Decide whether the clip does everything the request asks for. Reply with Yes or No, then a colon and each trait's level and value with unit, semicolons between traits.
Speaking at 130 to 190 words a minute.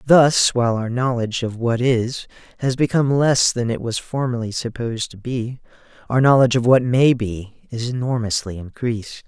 Yes: average, 170 wpm